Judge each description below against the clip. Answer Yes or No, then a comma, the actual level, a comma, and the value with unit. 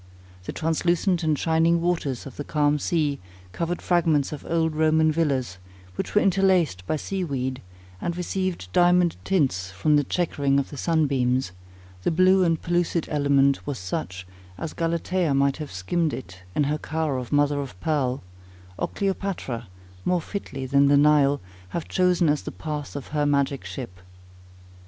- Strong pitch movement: No, average, 3.7 semitones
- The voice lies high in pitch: No, medium, 150 Hz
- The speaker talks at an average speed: Yes, average, 160 wpm